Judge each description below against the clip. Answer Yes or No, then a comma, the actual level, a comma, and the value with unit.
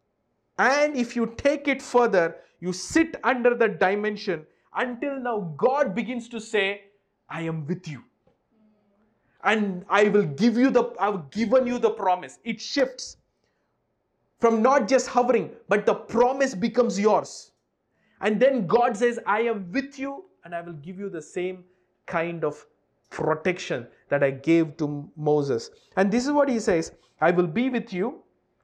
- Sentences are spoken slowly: No, average, 165 wpm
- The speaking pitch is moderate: No, high, 215 Hz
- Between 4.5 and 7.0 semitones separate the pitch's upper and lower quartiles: Yes, average, 5.2 semitones